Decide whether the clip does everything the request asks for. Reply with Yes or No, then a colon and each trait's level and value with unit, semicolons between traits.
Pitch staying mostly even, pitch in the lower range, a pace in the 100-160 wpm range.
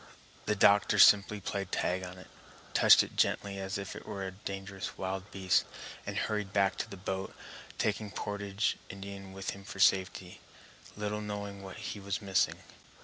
No: narrow, 1.1 semitones; low, 100 Hz; average, 175 wpm